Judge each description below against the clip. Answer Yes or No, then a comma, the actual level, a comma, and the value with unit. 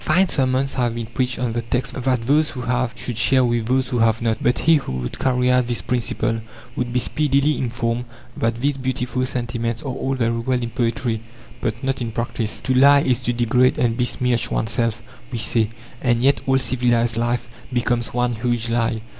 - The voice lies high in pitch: No, low, 120 Hz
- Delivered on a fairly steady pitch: Yes, narrow, 1.8 semitones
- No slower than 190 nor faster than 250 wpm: Yes, average, 200 wpm